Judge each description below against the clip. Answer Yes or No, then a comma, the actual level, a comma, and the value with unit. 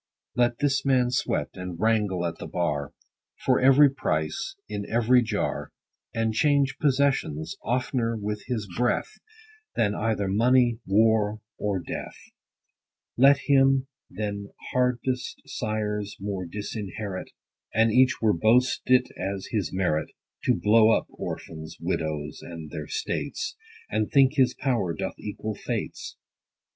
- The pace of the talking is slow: Yes, slow, 130 wpm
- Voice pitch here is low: Yes, low, 110 Hz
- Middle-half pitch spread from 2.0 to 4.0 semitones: No, average, 4.5 semitones